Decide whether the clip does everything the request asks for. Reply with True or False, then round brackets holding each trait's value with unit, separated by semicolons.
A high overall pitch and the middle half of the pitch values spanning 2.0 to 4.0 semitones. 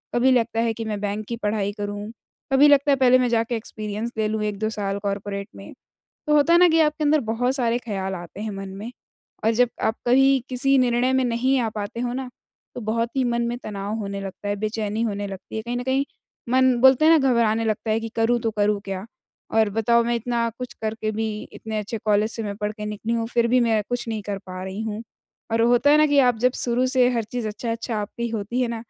True (225 Hz; 2.8 semitones)